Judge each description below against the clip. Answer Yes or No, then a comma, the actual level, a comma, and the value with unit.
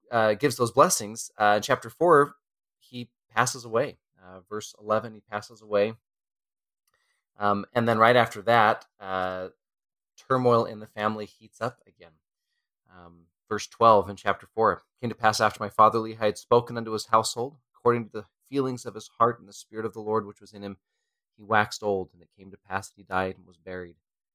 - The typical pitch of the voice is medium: No, low, 110 Hz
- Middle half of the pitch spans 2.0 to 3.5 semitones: Yes, average, 2.8 semitones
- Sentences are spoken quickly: No, average, 195 wpm